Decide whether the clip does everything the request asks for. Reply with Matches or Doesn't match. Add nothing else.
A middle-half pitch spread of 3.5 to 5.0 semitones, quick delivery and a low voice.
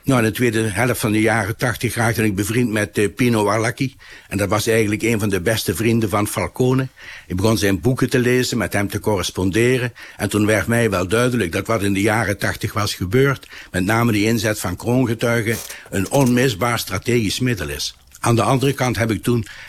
Doesn't match